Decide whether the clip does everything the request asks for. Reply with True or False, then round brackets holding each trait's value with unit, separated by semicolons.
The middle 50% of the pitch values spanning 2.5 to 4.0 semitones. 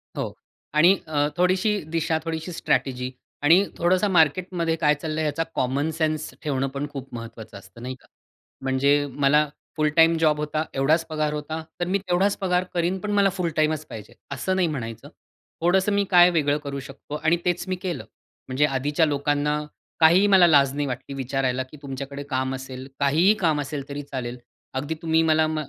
True (3.6 semitones)